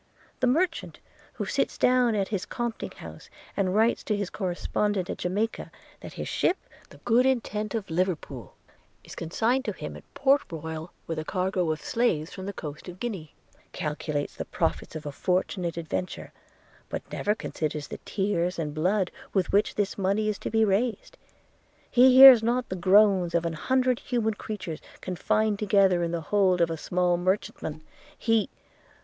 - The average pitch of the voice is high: Yes, high, 195 Hz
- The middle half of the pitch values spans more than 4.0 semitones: Yes, average, 4.6 semitones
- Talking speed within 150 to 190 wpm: Yes, average, 175 wpm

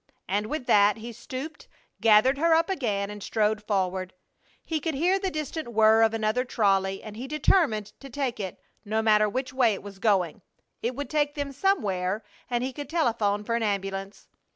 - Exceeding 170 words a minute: Yes, average, 190 wpm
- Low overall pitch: No, high, 225 Hz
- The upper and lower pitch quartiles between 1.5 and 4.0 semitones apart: No, average, 5.3 semitones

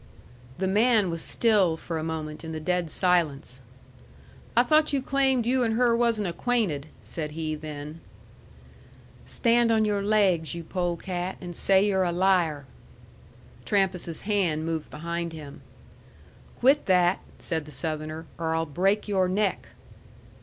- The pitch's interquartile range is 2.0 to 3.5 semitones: No, average, 4.6 semitones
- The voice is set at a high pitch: No, medium, 180 Hz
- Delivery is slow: No, average, 145 wpm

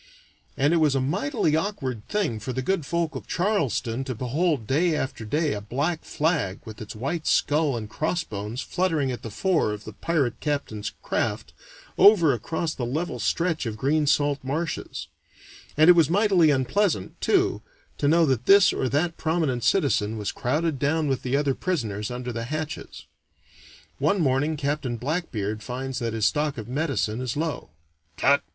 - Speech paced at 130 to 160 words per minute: No, average, 170 wpm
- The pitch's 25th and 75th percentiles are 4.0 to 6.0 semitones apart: Yes, average, 5.0 semitones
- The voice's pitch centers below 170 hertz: Yes, medium, 140 Hz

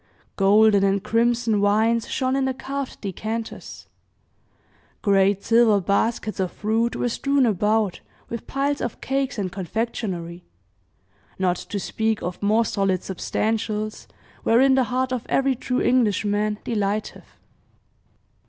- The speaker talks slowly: Yes, slow, 125 wpm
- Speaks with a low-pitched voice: No, high, 220 Hz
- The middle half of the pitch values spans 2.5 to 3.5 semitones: Yes, average, 3.1 semitones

